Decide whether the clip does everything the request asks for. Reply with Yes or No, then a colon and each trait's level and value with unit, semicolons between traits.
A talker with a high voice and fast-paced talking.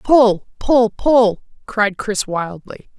No: high, 220 Hz; slow, 120 wpm